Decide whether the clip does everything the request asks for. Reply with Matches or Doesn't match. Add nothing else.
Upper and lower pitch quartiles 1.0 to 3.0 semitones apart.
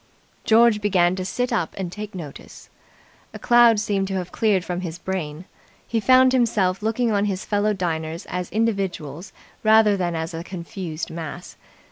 Doesn't match